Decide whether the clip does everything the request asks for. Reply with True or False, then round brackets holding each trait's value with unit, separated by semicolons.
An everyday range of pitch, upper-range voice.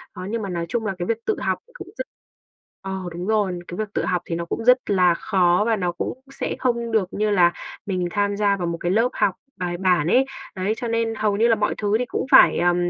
True (3.9 semitones; 200 Hz)